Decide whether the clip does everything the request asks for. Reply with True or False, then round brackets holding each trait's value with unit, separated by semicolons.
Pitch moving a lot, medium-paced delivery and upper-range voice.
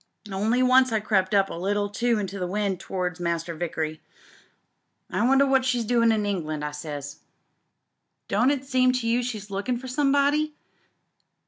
True (5.8 semitones; 165 wpm; 210 Hz)